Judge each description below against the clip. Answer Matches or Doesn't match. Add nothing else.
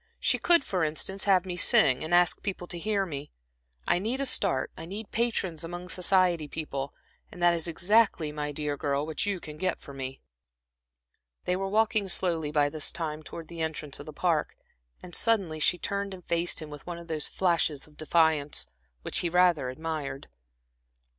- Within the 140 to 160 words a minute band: Doesn't match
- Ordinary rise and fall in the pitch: Matches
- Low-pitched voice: Doesn't match